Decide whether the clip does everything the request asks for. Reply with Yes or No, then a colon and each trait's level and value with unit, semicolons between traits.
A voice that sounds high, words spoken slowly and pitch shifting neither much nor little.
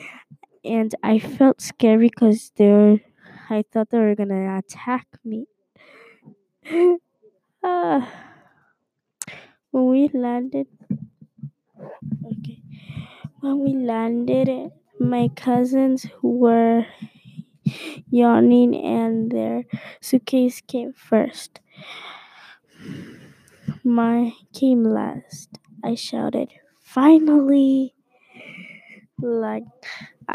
Yes: high, 240 Hz; slow, 75 wpm; average, 3.7 semitones